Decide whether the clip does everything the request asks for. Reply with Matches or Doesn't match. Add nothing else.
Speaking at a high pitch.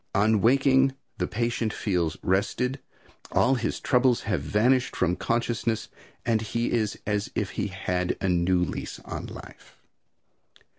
Doesn't match